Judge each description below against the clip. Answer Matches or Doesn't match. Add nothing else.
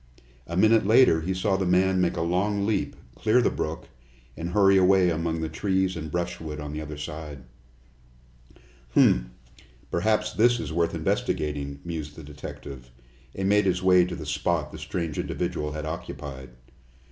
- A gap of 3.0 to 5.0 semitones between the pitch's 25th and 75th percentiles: Matches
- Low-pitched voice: Matches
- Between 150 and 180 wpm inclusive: Matches